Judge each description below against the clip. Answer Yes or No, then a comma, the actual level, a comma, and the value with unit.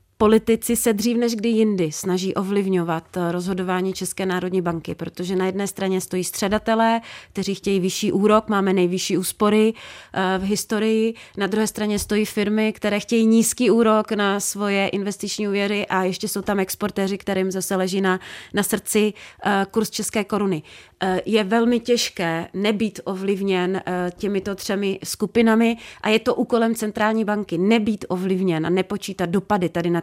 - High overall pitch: Yes, high, 200 Hz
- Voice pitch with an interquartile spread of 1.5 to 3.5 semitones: Yes, narrow, 2.5 semitones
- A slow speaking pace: No, average, 150 wpm